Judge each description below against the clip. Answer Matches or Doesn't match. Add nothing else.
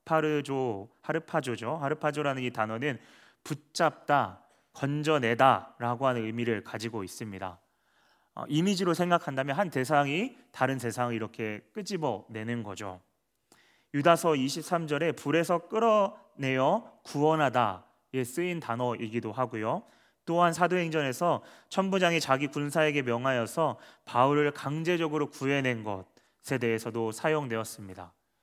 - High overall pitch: Doesn't match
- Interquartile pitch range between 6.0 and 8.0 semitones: Doesn't match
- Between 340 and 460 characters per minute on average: Doesn't match